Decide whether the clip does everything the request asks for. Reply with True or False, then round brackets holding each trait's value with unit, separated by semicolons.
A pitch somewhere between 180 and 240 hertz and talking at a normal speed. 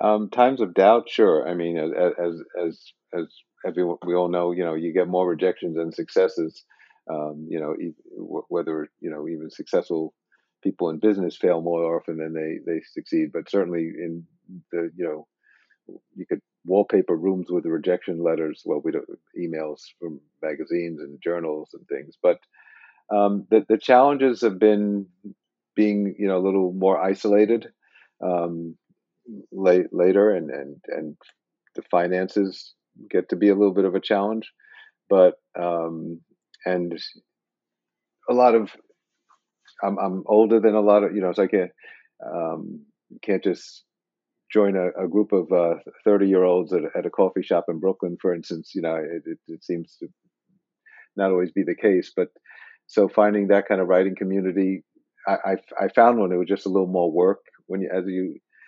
False (95 Hz; 175 wpm)